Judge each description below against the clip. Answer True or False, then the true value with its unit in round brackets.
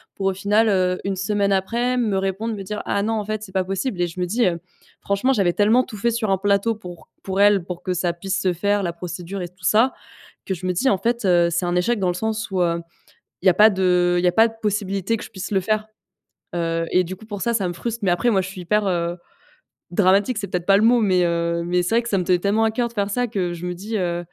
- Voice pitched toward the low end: False (195 Hz)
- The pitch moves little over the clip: False (3.1 semitones)